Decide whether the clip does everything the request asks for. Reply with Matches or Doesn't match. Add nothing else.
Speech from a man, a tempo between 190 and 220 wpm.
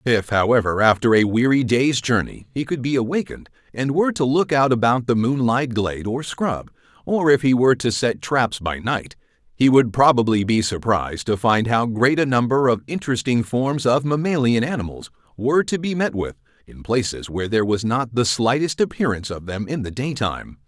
Matches